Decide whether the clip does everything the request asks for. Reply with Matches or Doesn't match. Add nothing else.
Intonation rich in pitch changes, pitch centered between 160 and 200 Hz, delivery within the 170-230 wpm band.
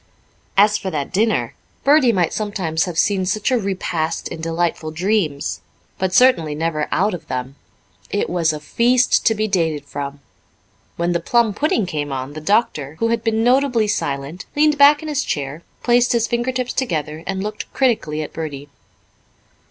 Matches